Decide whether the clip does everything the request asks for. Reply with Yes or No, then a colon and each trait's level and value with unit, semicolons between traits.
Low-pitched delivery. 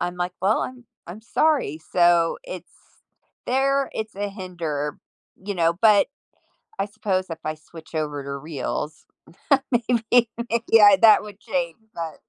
No: high, 190 Hz